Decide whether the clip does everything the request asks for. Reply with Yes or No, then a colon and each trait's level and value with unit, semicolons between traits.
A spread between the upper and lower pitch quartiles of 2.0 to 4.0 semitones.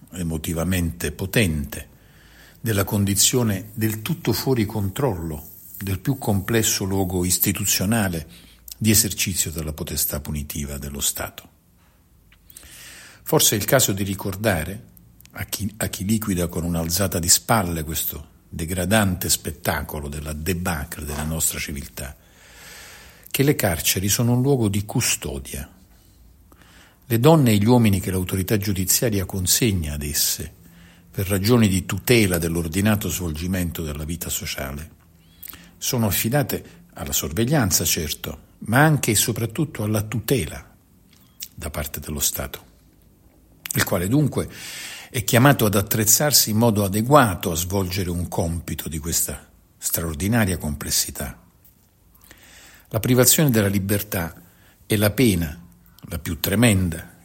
No: average, 4.6 semitones